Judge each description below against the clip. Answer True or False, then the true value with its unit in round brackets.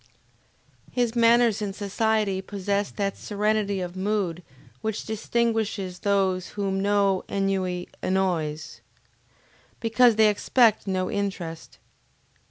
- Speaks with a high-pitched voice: True (200 Hz)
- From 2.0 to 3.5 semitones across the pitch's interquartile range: True (2.5 semitones)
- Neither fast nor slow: False (100 wpm)